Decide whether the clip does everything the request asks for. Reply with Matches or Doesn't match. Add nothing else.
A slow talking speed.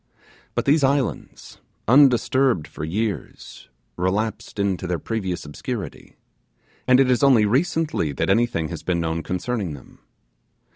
Matches